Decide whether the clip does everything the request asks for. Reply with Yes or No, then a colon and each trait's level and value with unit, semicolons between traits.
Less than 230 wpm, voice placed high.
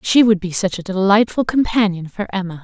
Yes: fast, 205 wpm; high, 200 Hz